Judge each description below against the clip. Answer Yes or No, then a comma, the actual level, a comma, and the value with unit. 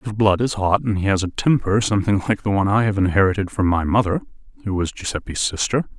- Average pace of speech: No, fast, 230 wpm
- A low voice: Yes, low, 105 Hz